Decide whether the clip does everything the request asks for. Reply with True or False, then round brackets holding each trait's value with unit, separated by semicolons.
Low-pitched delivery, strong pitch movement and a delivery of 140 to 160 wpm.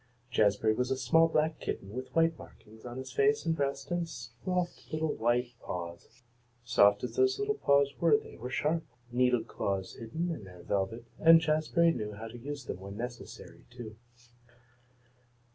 False (125 Hz; 6.4 semitones; 170 wpm)